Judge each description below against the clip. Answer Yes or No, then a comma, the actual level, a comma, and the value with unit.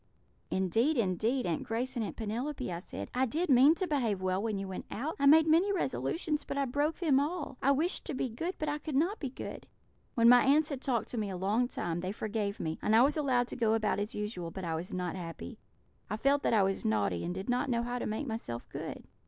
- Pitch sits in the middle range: No, high, 240 Hz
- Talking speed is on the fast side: Yes, fast, 250 wpm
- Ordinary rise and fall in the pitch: No, wide, 6.6 semitones